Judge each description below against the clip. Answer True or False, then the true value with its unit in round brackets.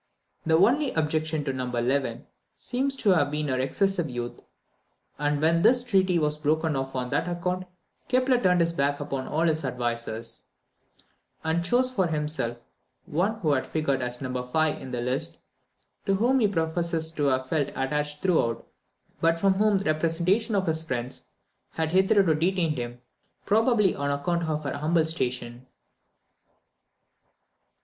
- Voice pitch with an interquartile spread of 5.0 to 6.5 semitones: True (5.3 semitones)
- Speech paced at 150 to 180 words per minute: True (155 wpm)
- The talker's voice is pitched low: False (160 Hz)